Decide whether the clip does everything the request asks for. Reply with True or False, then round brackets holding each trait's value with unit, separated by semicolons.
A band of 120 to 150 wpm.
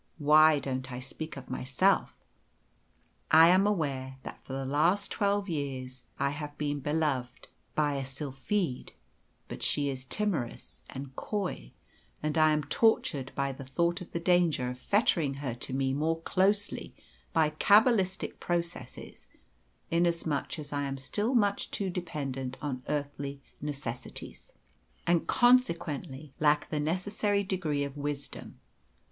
True (140 wpm)